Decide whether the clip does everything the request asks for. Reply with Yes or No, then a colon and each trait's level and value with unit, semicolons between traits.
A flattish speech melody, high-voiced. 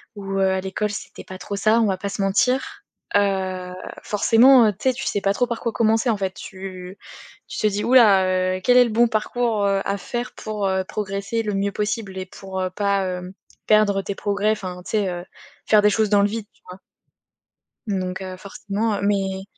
Yes: narrow, 2.2 semitones; high, 200 Hz